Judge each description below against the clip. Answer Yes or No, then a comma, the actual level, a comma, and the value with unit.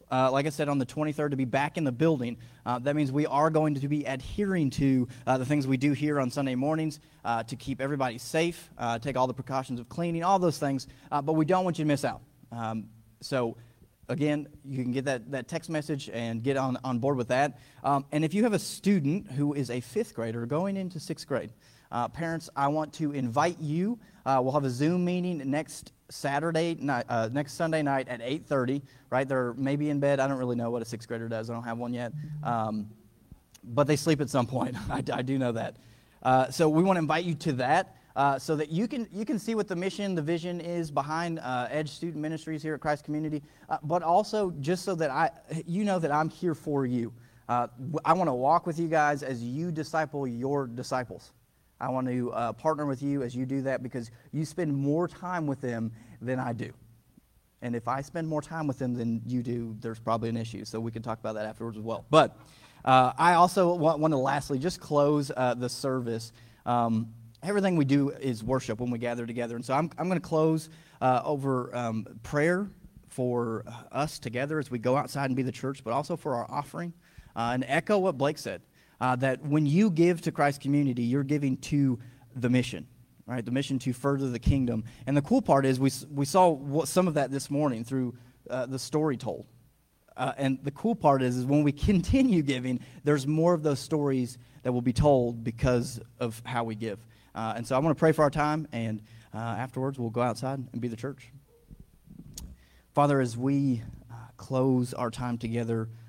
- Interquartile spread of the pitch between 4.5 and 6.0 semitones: No, average, 4.0 semitones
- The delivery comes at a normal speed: No, fast, 225 wpm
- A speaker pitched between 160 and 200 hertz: No, low, 135 Hz